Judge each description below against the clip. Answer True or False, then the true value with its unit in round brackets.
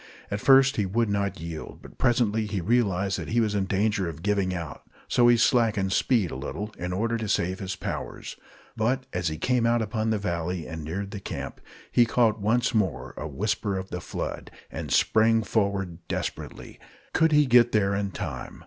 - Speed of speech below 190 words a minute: False (195 wpm)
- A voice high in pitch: False (105 Hz)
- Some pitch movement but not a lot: True (3.7 semitones)